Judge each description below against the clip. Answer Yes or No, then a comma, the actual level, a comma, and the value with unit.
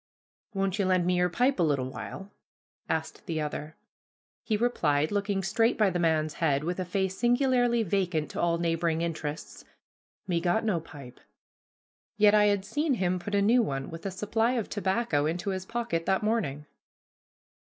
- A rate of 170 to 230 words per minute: Yes, average, 175 wpm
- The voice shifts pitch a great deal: No, average, 4.5 semitones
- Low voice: No, medium, 185 Hz